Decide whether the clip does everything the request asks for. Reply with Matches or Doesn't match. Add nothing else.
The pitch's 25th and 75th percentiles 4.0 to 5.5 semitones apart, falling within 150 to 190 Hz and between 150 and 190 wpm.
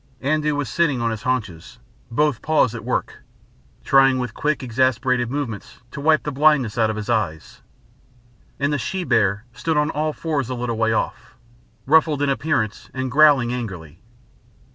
Doesn't match